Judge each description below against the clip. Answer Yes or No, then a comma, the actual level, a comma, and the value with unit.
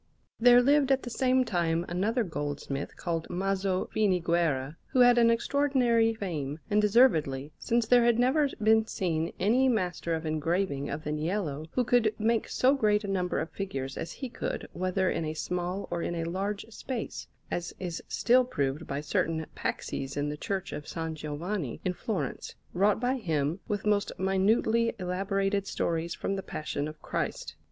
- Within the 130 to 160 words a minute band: No, average, 175 wpm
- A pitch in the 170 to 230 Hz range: Yes, high, 190 Hz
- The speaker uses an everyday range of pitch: No, wide, 5.7 semitones